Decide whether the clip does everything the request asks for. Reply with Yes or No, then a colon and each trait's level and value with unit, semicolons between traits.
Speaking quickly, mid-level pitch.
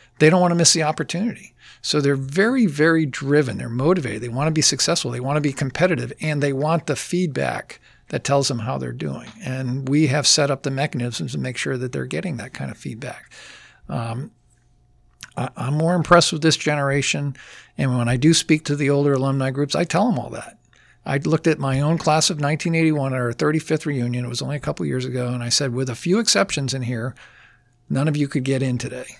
Yes: fast, 225 wpm; medium, 145 Hz